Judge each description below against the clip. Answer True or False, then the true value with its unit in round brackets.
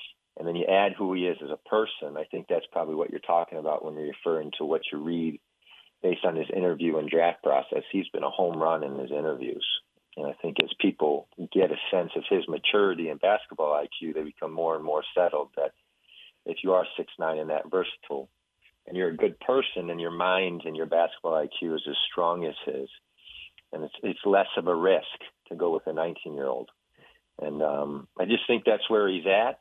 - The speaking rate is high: True (220 wpm)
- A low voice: True (85 Hz)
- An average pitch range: True (3.5 semitones)